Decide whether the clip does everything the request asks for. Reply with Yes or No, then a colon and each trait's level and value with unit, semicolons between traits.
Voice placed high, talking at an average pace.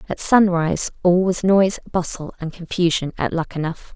No: medium, 175 Hz; average, 150 wpm